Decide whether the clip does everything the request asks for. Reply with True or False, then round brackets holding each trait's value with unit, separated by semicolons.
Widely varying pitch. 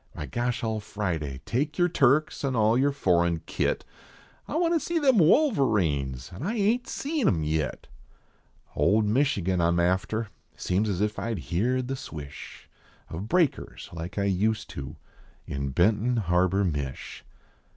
True (8.0 semitones)